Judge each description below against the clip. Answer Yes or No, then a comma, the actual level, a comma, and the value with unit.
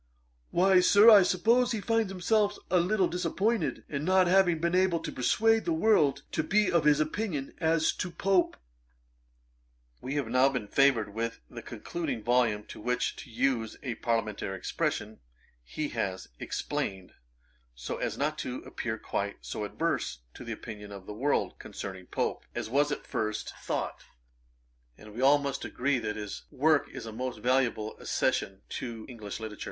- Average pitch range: No, wide, 8.2 semitones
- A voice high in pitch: No, low, 135 Hz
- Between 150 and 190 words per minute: Yes, average, 170 wpm